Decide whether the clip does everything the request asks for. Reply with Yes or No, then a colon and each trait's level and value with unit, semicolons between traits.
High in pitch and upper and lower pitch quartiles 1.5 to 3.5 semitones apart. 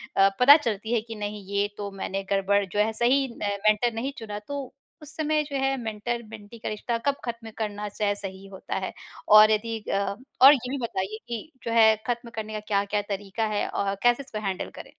Yes: high, 215 Hz; average, 2.8 semitones